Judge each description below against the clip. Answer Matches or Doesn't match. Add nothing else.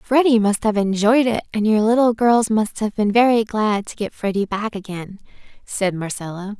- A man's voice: Doesn't match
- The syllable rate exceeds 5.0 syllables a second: Doesn't match